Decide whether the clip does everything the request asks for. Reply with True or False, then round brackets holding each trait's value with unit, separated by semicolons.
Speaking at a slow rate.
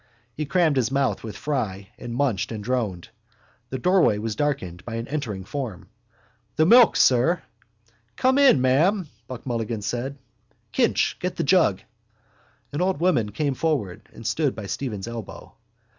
False (155 wpm)